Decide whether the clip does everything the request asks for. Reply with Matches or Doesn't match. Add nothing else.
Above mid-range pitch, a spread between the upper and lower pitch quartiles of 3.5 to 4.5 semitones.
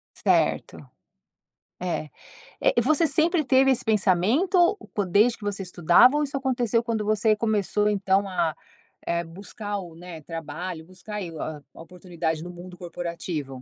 Doesn't match